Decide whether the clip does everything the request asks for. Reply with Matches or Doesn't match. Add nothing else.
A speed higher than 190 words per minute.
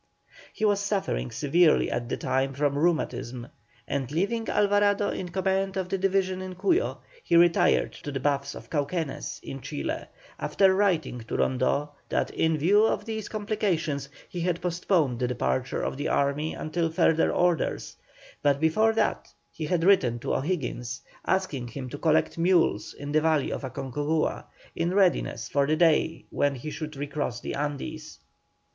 Doesn't match